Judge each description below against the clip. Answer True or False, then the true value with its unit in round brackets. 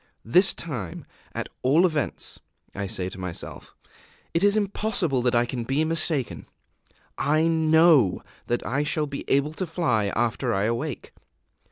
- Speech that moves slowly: False (150 wpm)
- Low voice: False (145 Hz)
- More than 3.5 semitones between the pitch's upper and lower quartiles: True (5.6 semitones)